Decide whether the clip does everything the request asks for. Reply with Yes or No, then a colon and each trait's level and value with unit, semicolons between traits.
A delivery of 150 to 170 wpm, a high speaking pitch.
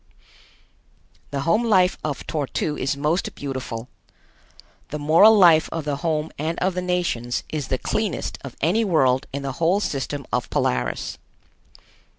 No: average, 155 wpm; medium, 155 Hz